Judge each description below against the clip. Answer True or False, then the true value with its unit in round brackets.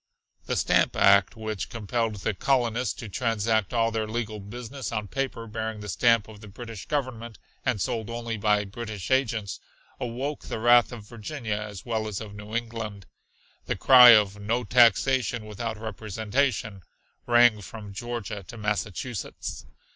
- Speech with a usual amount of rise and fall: False (2.2 semitones)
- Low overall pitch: True (110 Hz)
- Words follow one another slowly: False (155 wpm)